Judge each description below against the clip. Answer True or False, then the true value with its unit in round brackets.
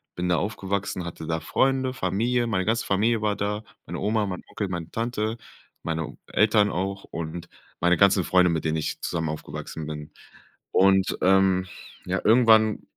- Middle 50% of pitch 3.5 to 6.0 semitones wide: True (3.9 semitones)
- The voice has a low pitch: True (95 Hz)